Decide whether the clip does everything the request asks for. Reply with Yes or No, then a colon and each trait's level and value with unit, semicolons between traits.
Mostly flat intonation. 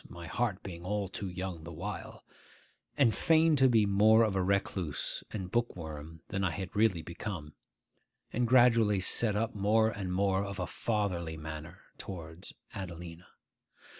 No: average, 4.2 semitones